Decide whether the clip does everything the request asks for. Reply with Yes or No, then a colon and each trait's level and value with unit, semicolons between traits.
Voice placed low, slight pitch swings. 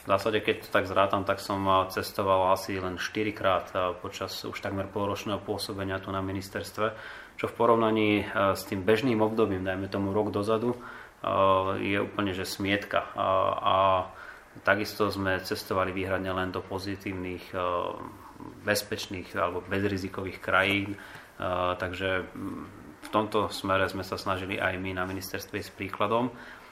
Yes: very low, 95 Hz; narrow, 1.6 semitones